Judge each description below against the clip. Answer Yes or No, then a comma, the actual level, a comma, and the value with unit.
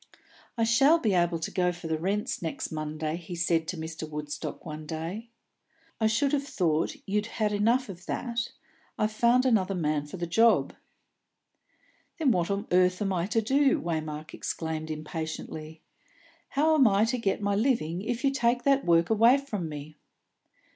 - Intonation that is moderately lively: No, wide, 6.3 semitones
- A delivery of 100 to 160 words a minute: No, average, 175 wpm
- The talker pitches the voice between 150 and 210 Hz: Yes, medium, 185 Hz